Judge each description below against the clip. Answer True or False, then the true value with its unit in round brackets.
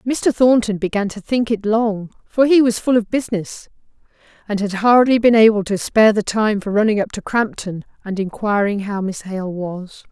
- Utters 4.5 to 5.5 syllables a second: True (4.9 syllables/s)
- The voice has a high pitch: True (210 Hz)